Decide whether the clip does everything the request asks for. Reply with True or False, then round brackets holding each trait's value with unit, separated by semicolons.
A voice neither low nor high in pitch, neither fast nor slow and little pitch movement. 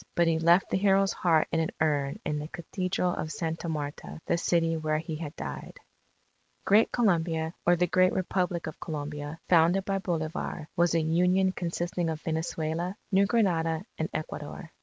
True (165 Hz; 170 wpm; 2.3 semitones)